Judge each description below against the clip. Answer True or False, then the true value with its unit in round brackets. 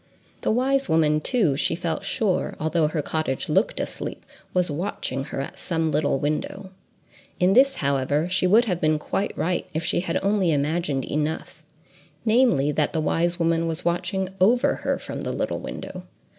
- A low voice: False (165 Hz)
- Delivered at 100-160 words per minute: False (170 wpm)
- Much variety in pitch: False (3.9 semitones)